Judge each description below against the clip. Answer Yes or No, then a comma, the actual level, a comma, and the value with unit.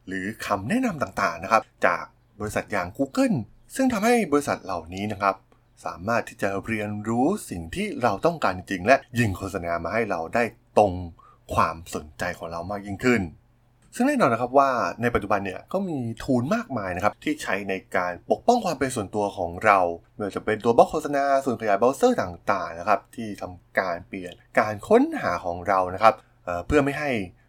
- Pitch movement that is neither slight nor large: No, wide, 6.3 semitones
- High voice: No, low, 110 Hz